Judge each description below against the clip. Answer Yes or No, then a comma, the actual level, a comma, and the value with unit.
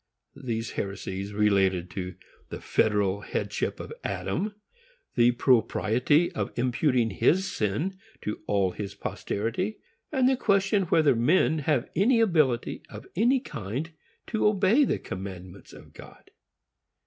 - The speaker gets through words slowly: Yes, slow, 125 wpm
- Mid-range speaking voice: No, low, 120 Hz